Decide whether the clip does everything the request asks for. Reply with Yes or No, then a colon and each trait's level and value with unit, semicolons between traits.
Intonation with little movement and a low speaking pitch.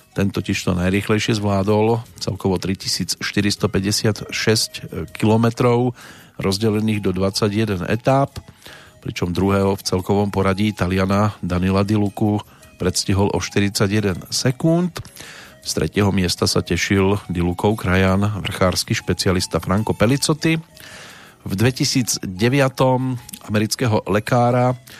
No: average, 3.3 semitones; low, 105 Hz